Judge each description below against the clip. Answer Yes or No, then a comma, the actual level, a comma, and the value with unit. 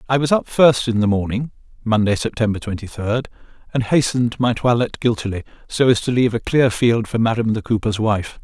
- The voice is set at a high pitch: No, low, 115 Hz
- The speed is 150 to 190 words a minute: No, average, 200 wpm